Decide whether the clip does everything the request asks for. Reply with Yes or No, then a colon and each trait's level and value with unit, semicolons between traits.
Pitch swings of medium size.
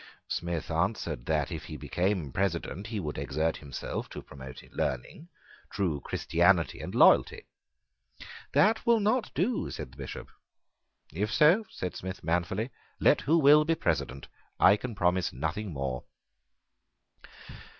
No: wide, 8.0 semitones